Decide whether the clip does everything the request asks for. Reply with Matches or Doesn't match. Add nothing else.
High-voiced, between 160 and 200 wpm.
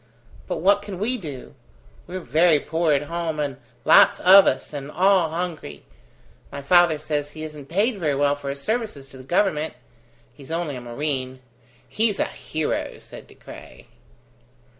Doesn't match